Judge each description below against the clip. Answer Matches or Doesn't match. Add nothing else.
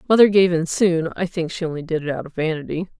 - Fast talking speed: Matches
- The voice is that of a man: Doesn't match